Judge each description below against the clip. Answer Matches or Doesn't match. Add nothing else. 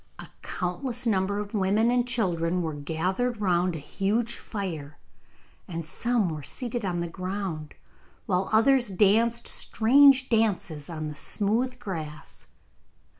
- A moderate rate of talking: Doesn't match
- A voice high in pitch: Matches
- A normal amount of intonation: Doesn't match